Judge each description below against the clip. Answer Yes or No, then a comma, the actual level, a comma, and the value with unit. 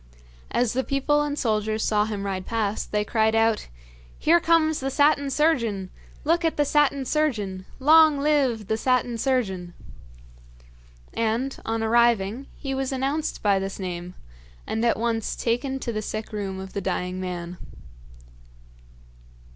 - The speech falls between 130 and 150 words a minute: Yes, average, 145 wpm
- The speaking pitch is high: Yes, high, 230 Hz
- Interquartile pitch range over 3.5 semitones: Yes, average, 5.2 semitones